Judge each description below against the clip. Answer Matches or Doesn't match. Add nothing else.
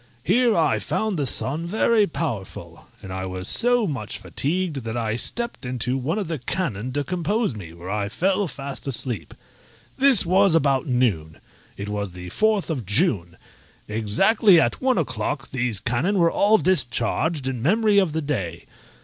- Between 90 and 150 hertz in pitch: Matches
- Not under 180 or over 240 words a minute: Doesn't match